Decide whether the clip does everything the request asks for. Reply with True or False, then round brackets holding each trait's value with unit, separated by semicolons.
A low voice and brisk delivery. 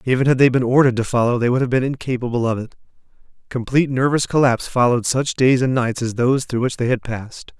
True (125 Hz; 230 wpm)